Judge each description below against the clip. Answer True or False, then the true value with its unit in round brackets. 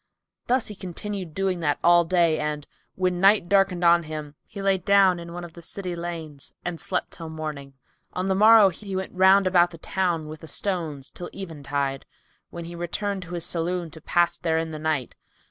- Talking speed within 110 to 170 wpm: False (195 wpm)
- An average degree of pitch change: True (3.0 semitones)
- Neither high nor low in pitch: True (175 Hz)